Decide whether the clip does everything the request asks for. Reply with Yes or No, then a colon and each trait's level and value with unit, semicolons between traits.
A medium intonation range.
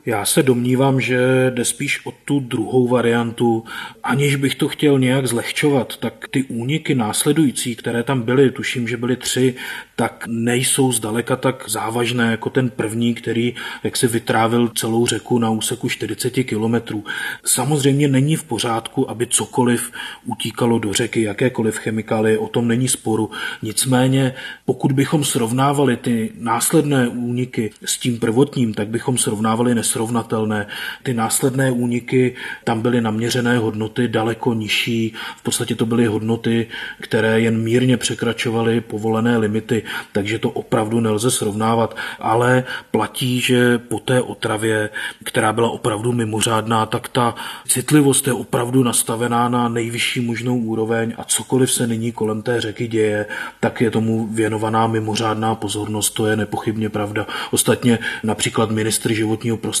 No: narrow, 2.2 semitones